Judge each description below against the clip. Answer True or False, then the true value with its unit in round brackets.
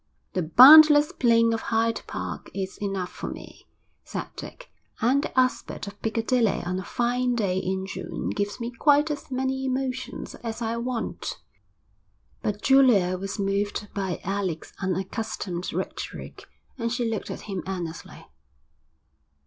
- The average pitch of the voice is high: True (225 Hz)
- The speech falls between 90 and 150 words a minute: True (140 wpm)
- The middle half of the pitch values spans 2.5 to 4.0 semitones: False (4.7 semitones)